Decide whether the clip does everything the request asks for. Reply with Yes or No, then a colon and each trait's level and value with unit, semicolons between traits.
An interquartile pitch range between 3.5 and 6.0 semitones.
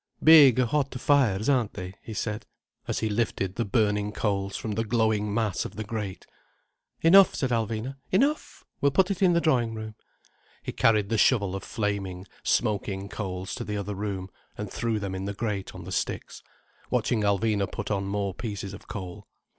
No: average, 3.1 semitones